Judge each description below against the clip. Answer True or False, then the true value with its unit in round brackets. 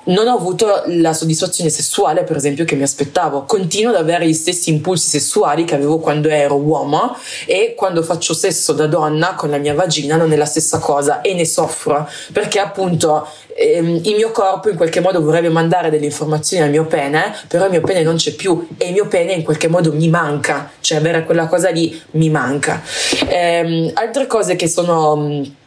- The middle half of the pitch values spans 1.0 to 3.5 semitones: True (2.9 semitones)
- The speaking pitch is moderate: True (165 Hz)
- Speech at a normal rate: False (200 wpm)